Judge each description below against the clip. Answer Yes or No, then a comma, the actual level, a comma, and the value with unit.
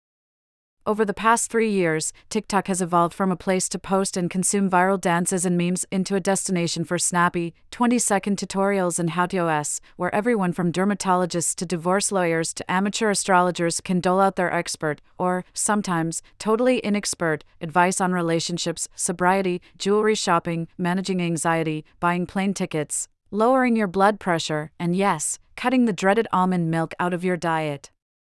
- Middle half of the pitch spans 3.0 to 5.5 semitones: No, narrow, 2.5 semitones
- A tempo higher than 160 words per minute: No, average, 155 wpm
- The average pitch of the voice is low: No, medium, 180 Hz